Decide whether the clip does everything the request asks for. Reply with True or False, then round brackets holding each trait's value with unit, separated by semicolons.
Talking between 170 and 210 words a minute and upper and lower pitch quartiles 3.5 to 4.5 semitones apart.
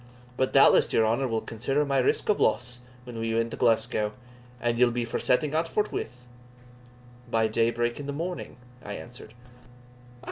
False (175 wpm; 3.0 semitones)